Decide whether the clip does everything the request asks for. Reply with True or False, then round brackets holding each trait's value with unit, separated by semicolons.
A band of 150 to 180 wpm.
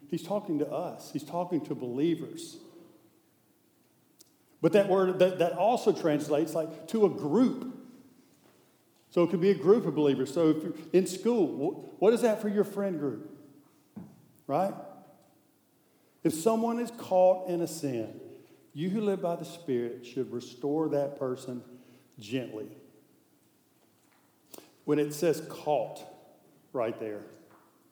False (140 wpm)